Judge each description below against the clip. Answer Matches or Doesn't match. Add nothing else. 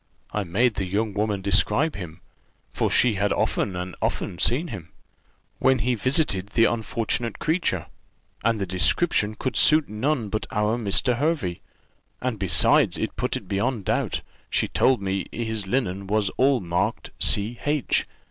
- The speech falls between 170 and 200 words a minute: Doesn't match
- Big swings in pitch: Doesn't match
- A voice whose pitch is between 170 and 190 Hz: Doesn't match